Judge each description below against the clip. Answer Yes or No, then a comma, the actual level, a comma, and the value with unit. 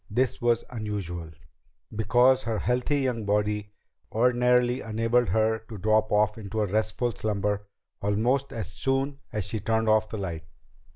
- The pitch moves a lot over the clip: No, average, 2.7 semitones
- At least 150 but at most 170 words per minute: No, average, 140 wpm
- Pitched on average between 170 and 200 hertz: No, low, 110 Hz